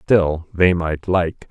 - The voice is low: Yes, very low, 85 Hz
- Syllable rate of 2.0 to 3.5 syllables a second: Yes, 2.8 syllables/s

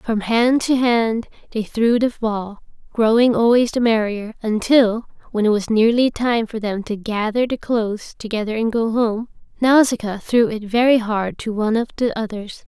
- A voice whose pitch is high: Yes, high, 225 Hz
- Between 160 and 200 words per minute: Yes, average, 180 wpm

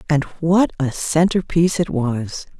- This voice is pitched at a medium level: Yes, medium, 160 Hz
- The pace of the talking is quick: No, average, 140 wpm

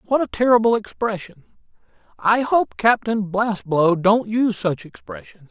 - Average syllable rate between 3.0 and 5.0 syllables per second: Yes, 4.6 syllables/s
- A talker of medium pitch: No, high, 195 Hz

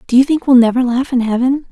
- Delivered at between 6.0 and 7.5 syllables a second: Yes, 6.5 syllables/s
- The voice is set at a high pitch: Yes, very high, 255 Hz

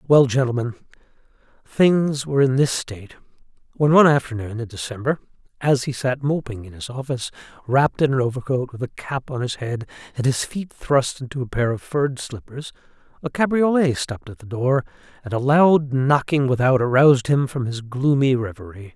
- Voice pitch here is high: No, low, 130 Hz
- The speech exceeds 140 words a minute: Yes, average, 175 wpm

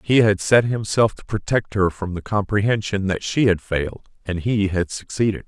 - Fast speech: No, average, 195 wpm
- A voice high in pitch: No, low, 100 Hz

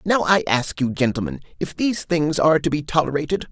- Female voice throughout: No, male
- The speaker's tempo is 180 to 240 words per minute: Yes, fast, 205 wpm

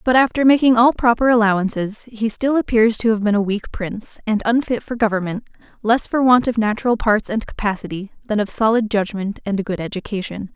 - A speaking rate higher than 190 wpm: Yes, average, 200 wpm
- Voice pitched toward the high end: Yes, high, 220 Hz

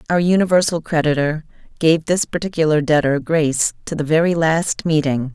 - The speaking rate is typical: Yes, average, 145 wpm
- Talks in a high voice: No, medium, 160 Hz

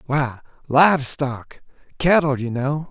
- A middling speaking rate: No, slow, 125 wpm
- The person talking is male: Yes, male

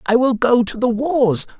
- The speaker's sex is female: No, male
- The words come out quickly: Yes, fast, 225 wpm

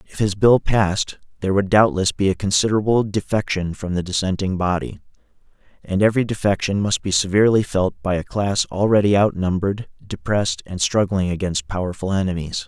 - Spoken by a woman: No, male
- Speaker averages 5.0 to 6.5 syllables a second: Yes, 5.8 syllables/s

